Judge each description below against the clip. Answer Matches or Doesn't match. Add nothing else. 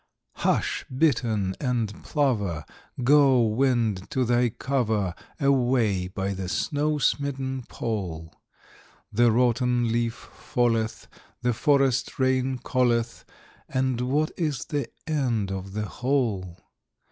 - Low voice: Matches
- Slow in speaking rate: Matches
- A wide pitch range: Doesn't match